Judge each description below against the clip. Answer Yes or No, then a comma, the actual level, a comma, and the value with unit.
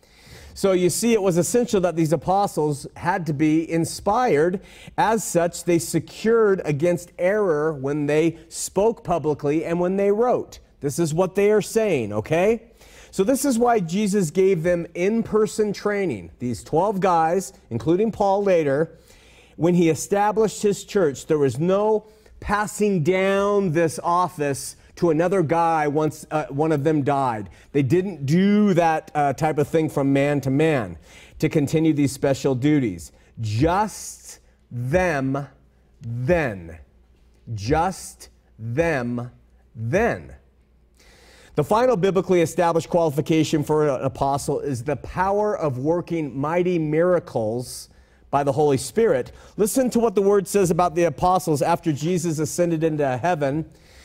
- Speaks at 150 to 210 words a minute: No, average, 140 wpm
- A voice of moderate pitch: Yes, medium, 165 Hz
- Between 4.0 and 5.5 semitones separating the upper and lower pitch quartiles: Yes, average, 5.2 semitones